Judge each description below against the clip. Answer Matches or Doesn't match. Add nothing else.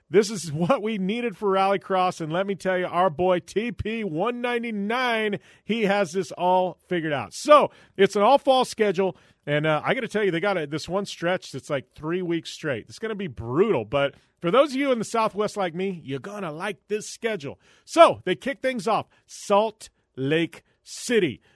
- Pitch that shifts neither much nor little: Matches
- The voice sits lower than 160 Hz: Doesn't match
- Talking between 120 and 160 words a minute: Doesn't match